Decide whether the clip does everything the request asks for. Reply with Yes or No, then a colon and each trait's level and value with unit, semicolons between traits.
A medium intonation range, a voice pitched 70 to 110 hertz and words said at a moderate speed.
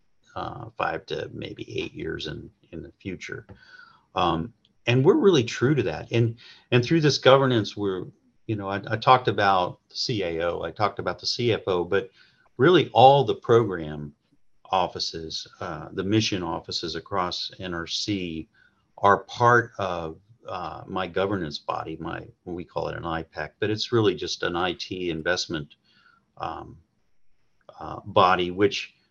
Yes: average, 4.9 semitones; low, 105 Hz; average, 150 wpm